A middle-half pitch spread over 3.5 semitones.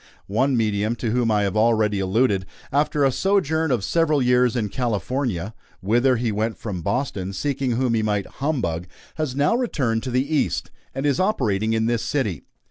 Yes: average, 4.5 semitones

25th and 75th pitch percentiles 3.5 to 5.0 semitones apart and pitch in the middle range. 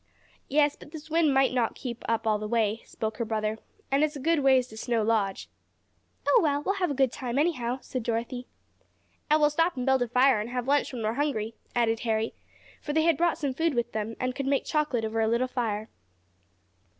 No: average, 4.4 semitones; very high, 255 Hz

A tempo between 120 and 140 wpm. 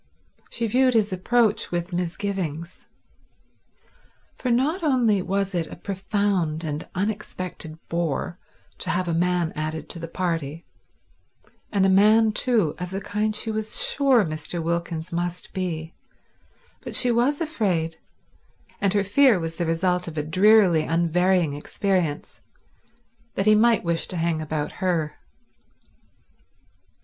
Yes: slow, 135 wpm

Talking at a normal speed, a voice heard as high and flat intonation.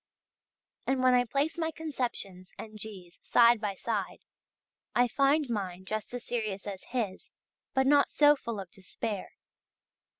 No: average, 145 wpm; high, 230 Hz; average, 5.1 semitones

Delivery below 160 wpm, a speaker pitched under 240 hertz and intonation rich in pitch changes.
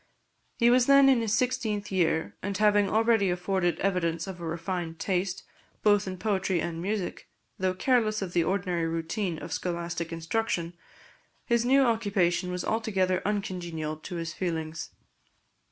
No: average, 150 wpm; medium, 185 Hz; average, 3.7 semitones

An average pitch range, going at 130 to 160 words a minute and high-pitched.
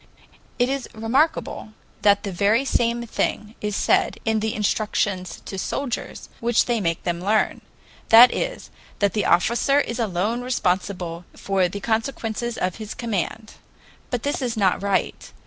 Yes: average, 3.3 semitones; average, 150 wpm; high, 220 Hz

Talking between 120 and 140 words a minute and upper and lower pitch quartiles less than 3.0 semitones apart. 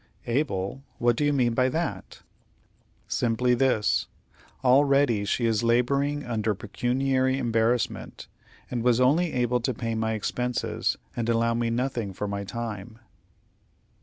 Yes: slow, 135 wpm; narrow, 2.6 semitones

